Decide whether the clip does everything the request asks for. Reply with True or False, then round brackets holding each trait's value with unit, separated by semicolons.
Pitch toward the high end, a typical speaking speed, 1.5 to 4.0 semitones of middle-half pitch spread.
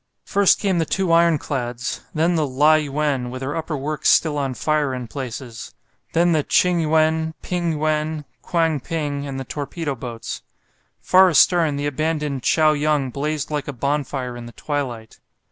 False (150 Hz; 165 wpm; 3.0 semitones)